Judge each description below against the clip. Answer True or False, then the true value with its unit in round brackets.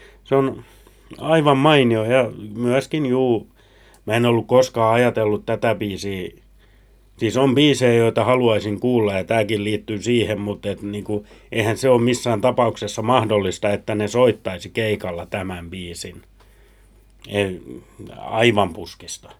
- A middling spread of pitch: True (3.0 semitones)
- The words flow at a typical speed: True (125 wpm)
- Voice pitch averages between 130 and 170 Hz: False (110 Hz)